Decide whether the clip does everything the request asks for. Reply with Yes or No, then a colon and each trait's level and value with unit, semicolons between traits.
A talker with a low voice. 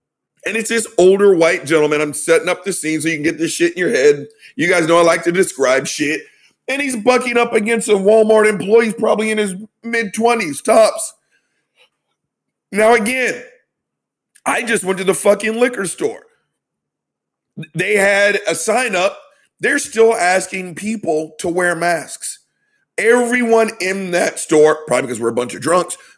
No: high, 205 Hz